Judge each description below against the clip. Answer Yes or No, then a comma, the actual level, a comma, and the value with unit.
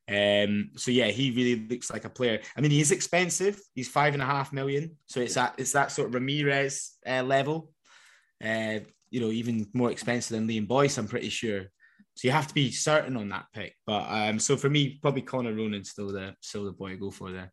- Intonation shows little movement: No, average, 4.4 semitones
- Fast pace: Yes, fast, 235 wpm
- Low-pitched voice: Yes, low, 125 Hz